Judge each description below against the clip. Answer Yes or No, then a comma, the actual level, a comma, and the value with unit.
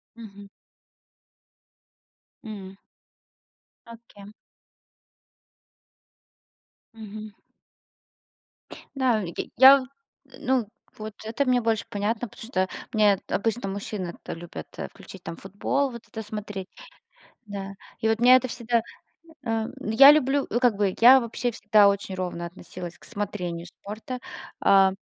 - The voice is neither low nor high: No, high, 215 Hz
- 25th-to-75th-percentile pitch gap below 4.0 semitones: Yes, average, 3.2 semitones